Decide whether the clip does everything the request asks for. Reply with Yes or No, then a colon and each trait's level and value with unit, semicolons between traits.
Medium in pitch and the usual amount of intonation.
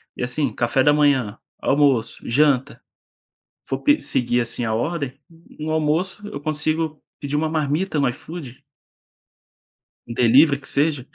Yes: medium, 145 Hz; average, 3.8 semitones